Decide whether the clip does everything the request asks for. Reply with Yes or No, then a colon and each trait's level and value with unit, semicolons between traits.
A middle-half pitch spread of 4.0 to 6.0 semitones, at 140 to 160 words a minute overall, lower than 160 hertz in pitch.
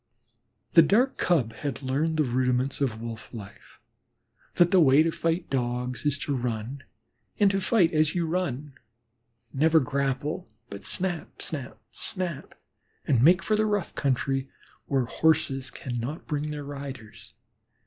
Yes: average, 4.5 semitones; average, 145 wpm; medium, 140 Hz